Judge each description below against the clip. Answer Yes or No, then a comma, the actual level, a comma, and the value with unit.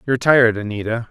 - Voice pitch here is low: Yes, low, 115 Hz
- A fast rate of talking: No, average, 165 wpm